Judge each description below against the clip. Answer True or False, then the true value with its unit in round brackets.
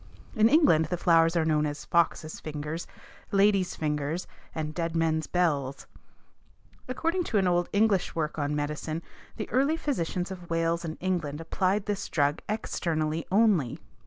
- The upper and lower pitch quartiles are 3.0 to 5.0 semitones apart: True (4.0 semitones)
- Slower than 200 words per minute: True (150 wpm)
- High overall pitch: False (165 Hz)